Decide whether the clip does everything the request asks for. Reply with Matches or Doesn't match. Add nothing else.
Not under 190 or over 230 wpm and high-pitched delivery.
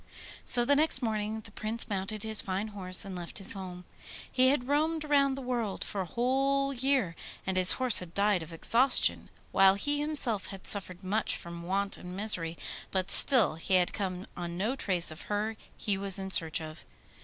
Matches